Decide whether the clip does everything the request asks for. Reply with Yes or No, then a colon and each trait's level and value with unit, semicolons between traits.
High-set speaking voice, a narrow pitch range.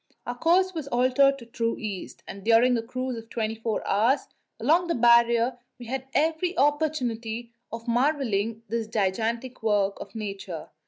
No: high, 235 Hz; average, 3.1 semitones